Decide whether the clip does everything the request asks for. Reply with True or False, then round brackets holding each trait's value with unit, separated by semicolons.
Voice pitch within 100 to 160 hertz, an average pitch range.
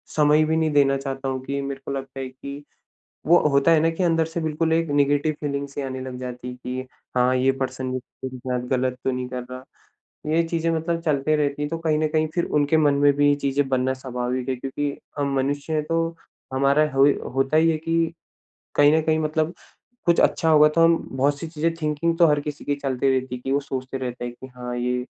True (140 Hz; 3.1 semitones)